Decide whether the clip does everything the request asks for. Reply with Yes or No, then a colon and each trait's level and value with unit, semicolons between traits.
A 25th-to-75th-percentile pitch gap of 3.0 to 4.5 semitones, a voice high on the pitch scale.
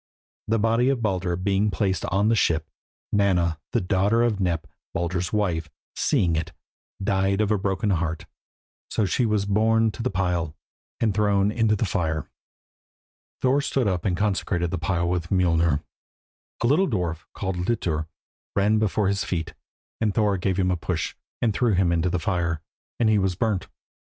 No: average, 3.5 semitones; very low, 95 Hz